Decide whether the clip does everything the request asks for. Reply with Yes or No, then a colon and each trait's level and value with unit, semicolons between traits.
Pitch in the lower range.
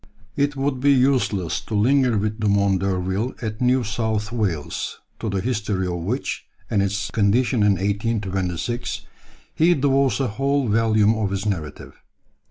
Yes: low, 110 Hz